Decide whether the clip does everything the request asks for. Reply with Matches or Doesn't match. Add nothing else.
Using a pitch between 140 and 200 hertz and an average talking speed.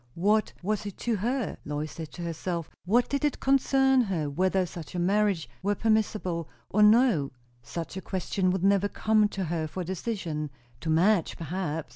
Matches